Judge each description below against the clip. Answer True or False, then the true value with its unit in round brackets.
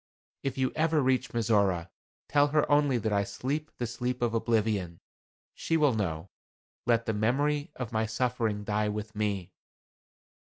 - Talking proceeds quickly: False (155 wpm)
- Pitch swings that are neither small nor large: True (4.2 semitones)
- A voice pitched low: True (115 Hz)